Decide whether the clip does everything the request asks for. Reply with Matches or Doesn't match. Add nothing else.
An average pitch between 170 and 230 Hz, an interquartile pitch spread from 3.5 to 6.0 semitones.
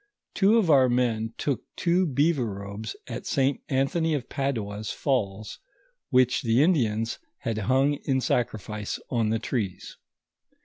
Doesn't match